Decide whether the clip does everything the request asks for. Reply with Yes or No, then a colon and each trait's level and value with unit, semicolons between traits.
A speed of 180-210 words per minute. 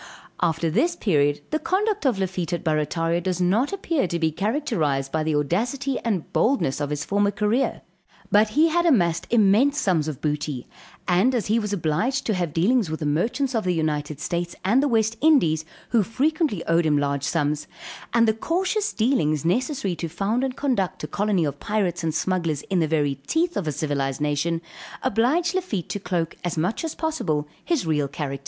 Yes: average, 190 wpm